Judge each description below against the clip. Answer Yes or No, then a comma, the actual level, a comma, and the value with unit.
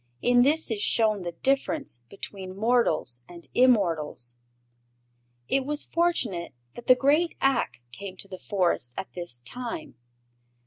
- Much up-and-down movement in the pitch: Yes, wide, 7.4 semitones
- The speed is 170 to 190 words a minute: No, slow, 135 wpm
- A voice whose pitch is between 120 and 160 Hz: No, high, 215 Hz